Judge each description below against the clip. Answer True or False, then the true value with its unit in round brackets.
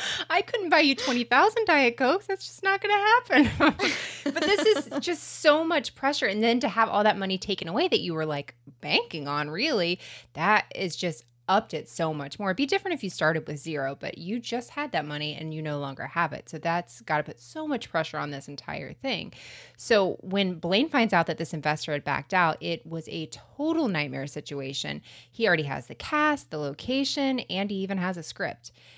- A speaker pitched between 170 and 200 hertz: True (185 Hz)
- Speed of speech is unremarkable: False (220 wpm)